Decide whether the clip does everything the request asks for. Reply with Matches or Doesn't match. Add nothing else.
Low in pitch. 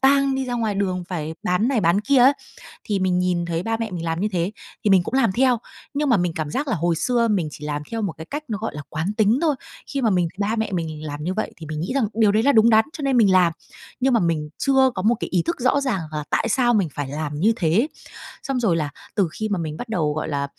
Doesn't match